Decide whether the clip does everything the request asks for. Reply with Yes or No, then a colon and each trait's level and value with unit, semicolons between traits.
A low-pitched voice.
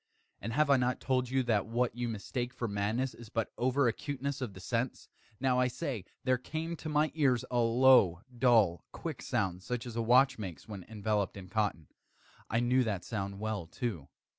Yes: low, 120 Hz